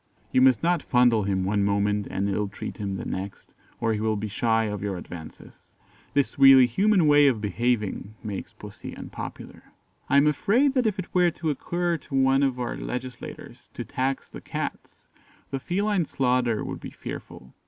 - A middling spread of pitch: No, wide, 6.0 semitones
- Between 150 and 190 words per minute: Yes, average, 180 wpm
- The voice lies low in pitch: Yes, low, 125 Hz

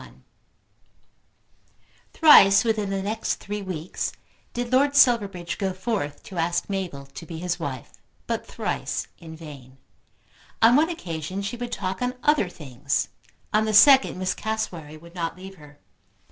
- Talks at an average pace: Yes, average, 150 wpm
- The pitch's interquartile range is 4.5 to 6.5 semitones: Yes, average, 5.2 semitones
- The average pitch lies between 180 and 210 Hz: Yes, high, 190 Hz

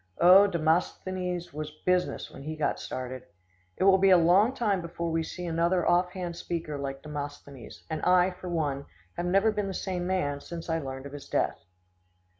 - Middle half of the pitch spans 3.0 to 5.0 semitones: Yes, average, 3.5 semitones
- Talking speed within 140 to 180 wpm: No, average, 190 wpm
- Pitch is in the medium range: Yes, medium, 170 Hz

